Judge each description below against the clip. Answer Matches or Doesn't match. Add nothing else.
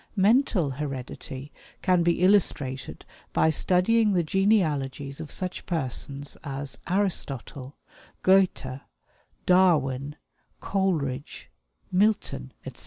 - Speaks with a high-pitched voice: Doesn't match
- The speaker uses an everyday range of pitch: Doesn't match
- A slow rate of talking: Matches